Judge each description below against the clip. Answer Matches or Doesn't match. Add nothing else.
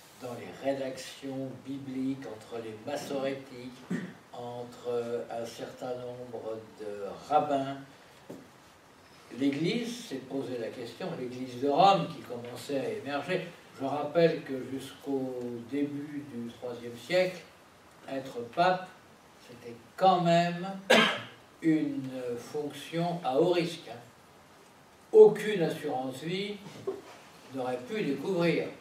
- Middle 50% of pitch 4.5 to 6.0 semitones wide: Matches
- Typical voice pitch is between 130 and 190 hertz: Matches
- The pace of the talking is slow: Matches